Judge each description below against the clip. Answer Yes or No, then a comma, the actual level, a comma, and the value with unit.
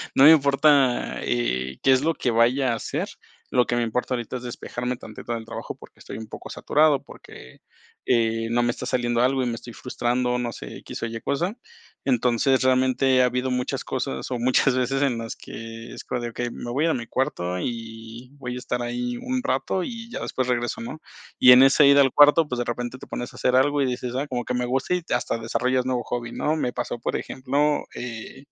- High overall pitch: No, low, 125 Hz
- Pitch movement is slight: Yes, narrow, 2.1 semitones